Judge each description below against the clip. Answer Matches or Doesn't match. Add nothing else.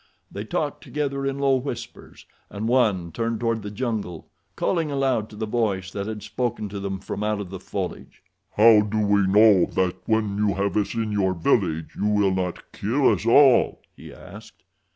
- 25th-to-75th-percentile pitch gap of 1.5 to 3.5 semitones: Matches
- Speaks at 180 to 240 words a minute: Matches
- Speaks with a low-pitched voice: Matches